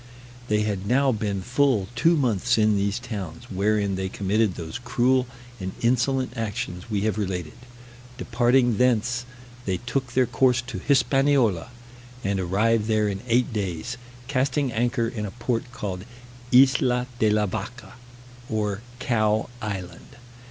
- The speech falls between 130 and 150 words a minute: Yes, average, 140 wpm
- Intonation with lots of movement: No, average, 3.7 semitones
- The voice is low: Yes, low, 115 Hz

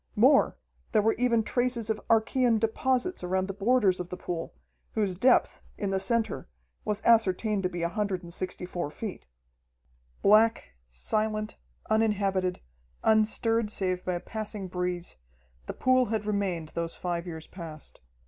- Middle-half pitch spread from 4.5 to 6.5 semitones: No, average, 3.6 semitones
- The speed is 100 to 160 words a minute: Yes, average, 140 wpm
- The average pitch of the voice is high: Yes, high, 205 Hz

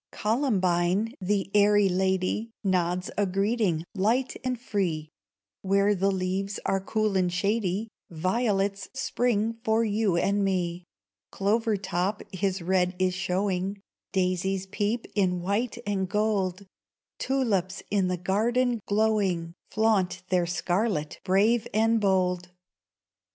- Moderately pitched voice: No, high, 195 Hz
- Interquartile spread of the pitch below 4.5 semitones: Yes, average, 2.8 semitones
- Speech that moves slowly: Yes, slow, 120 wpm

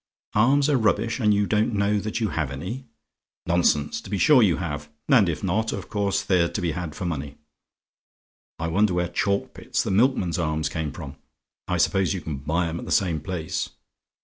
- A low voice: Yes, very low, 90 Hz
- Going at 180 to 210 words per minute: Yes, average, 200 wpm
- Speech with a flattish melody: No, average, 4.4 semitones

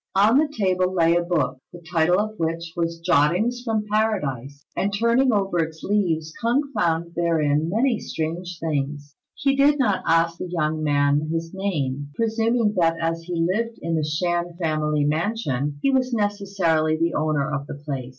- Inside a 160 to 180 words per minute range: Yes, average, 170 wpm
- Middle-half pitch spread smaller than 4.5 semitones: No, average, 4.9 semitones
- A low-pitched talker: No, medium, 170 Hz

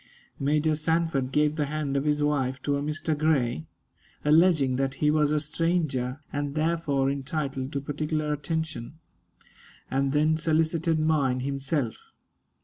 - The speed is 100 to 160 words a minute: Yes, average, 140 wpm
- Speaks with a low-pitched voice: No, medium, 150 Hz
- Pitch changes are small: Yes, narrow, 2.3 semitones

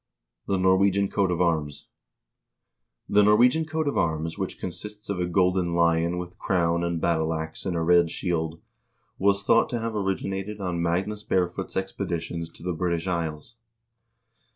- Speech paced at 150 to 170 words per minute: Yes, average, 160 wpm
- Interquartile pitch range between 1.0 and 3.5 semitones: Yes, average, 2.8 semitones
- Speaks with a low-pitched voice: Yes, very low, 90 Hz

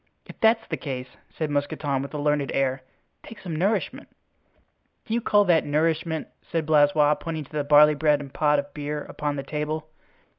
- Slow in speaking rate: No, average, 185 wpm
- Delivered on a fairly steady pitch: Yes, narrow, 1.7 semitones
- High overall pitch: No, medium, 150 Hz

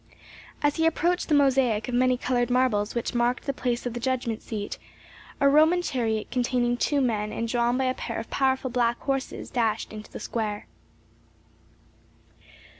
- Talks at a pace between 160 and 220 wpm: Yes, average, 170 wpm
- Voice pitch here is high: Yes, high, 245 Hz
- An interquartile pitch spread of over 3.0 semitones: No, narrow, 2.4 semitones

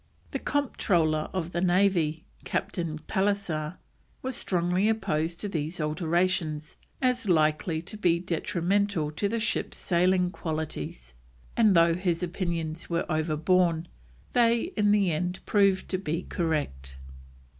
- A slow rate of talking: Yes, slow, 125 wpm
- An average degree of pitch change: Yes, average, 3.7 semitones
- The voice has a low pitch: No, medium, 175 Hz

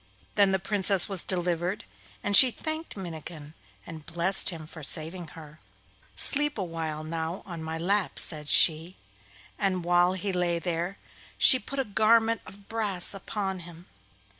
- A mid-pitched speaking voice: Yes, medium, 180 Hz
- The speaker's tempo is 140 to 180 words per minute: Yes, average, 155 wpm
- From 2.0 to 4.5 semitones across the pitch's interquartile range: Yes, average, 3.4 semitones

